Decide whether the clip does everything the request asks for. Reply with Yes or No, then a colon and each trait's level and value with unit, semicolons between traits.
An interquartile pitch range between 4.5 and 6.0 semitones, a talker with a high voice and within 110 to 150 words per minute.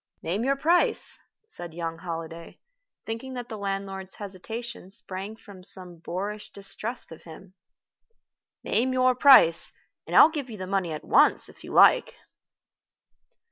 Yes: average, 5.2 semitones; high, 195 Hz; average, 140 wpm